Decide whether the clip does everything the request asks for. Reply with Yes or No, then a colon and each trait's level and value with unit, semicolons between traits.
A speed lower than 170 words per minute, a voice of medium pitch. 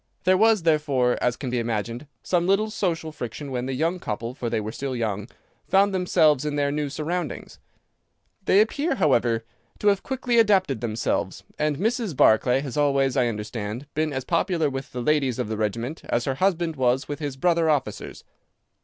No: average, 185 wpm; medium, 145 Hz